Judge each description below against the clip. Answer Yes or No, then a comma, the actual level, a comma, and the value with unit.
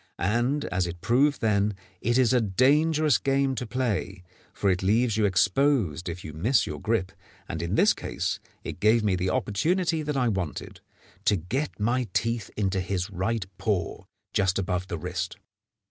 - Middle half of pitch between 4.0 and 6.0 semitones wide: Yes, wide, 5.5 semitones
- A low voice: Yes, low, 105 Hz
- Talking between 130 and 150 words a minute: No, average, 175 wpm